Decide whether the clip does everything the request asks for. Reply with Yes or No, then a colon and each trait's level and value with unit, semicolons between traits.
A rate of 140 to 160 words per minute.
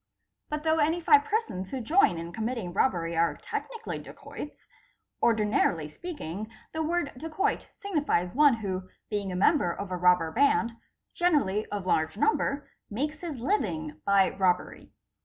Yes: average, 150 wpm